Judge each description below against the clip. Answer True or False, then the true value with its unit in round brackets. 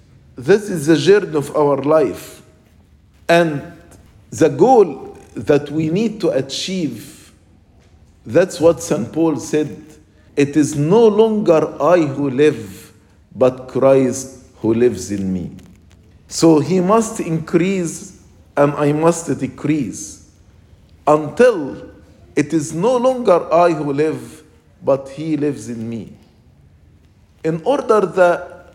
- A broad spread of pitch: True (7.2 semitones)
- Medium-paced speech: False (120 wpm)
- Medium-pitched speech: True (150 Hz)